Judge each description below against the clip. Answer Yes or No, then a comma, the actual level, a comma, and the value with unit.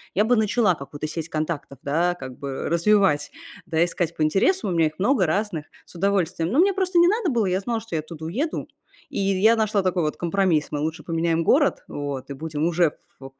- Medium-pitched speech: Yes, medium, 175 Hz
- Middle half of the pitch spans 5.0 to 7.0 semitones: Yes, average, 5.3 semitones